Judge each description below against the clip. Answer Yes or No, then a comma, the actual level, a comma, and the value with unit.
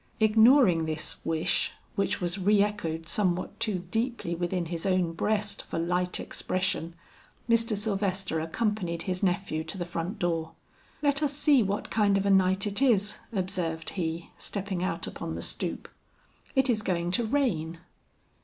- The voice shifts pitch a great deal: No, average, 3.8 semitones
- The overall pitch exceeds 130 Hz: Yes, high, 190 Hz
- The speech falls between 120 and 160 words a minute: Yes, average, 155 wpm